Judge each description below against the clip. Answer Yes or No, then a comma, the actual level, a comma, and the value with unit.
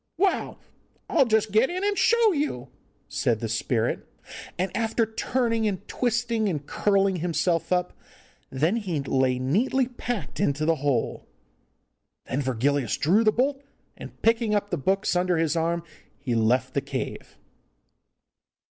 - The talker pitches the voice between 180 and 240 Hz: Yes, medium, 185 Hz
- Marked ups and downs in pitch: Yes, wide, 8.5 semitones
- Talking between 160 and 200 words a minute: No, average, 145 wpm